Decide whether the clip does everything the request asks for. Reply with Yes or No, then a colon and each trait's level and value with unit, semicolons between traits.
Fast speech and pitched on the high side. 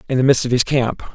No: fast, 315 wpm; low, 125 Hz